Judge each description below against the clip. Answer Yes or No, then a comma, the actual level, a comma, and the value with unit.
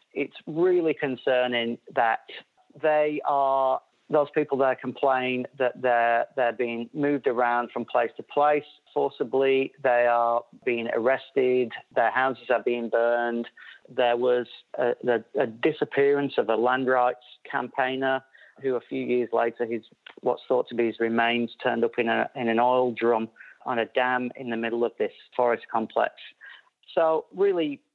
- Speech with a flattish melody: Yes, narrow, 2.3 semitones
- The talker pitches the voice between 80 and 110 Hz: No, low, 125 Hz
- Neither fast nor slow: Yes, average, 160 wpm